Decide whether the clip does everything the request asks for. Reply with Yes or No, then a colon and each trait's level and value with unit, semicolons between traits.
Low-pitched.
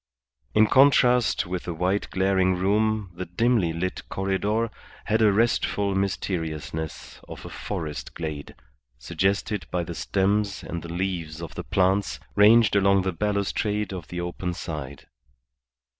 Yes: very low, 95 Hz